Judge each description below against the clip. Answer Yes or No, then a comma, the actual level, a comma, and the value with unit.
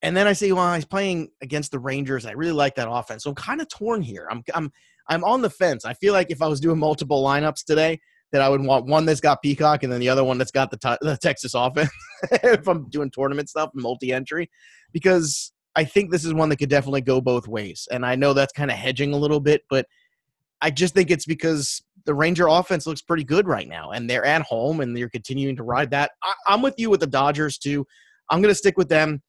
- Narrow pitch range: No, average, 4.1 semitones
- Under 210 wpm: No, fast, 250 wpm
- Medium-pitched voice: Yes, medium, 150 Hz